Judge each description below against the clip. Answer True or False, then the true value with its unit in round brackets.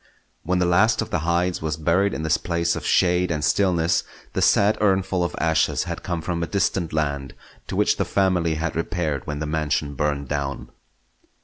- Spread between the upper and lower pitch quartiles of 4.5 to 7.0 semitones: False (2.8 semitones)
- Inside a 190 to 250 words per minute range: True (195 wpm)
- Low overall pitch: True (85 Hz)